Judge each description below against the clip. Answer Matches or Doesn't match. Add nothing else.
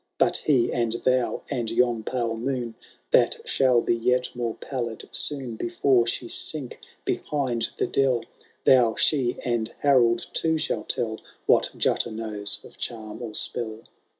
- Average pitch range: Doesn't match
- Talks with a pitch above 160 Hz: Doesn't match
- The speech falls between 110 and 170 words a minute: Matches